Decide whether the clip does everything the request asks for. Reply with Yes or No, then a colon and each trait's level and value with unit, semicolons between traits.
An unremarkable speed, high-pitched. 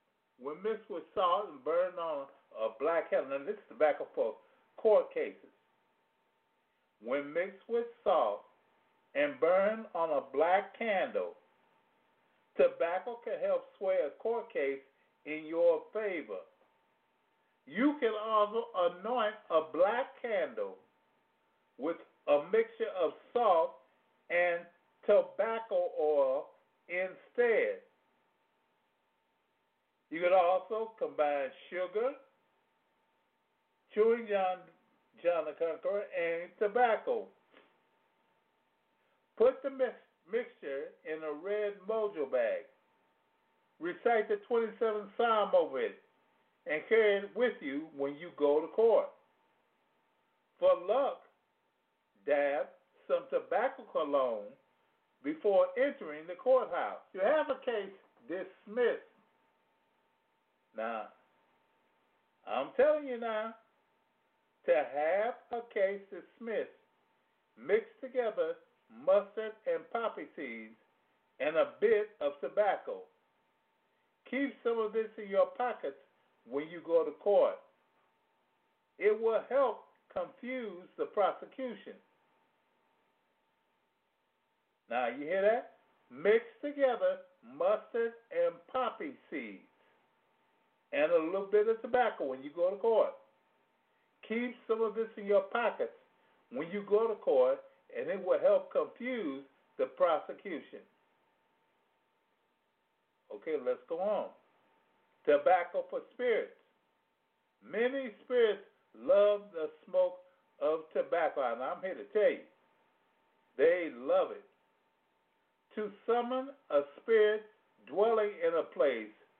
No: slow, 110 wpm; high, 240 Hz